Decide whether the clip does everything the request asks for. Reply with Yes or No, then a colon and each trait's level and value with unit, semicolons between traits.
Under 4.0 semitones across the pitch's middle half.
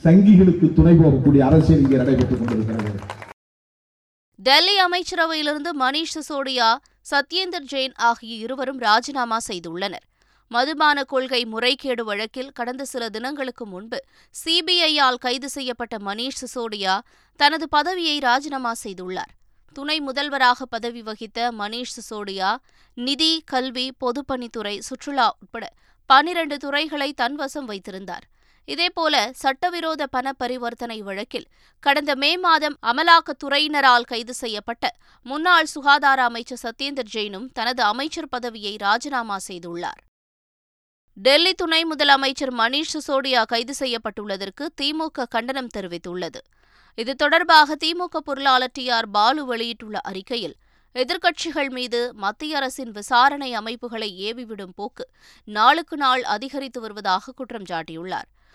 No: average, 4.5 semitones